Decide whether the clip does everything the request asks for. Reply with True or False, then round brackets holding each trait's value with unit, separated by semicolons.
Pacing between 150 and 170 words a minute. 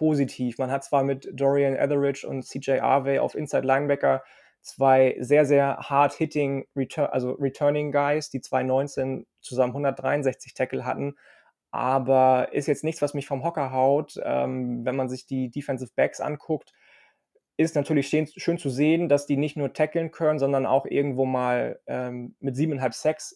True (165 wpm)